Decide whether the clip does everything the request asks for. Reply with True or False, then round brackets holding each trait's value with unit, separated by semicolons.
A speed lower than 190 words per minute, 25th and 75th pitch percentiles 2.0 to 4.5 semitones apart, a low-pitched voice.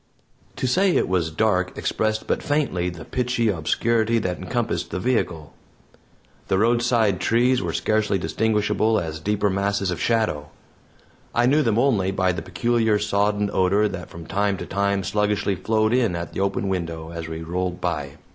True (165 wpm; 3.8 semitones; 100 Hz)